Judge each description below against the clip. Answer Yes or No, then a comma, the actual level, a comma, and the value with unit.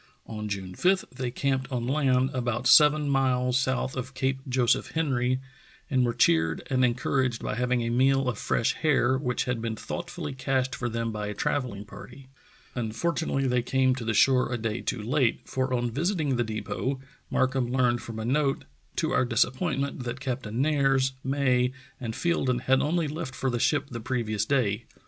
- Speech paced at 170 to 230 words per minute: Yes, average, 185 wpm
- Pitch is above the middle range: No, low, 125 Hz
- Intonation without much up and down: Yes, narrow, 2.2 semitones